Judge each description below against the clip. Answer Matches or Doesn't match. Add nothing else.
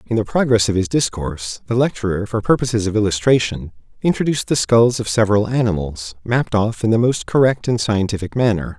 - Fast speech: Doesn't match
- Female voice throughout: Doesn't match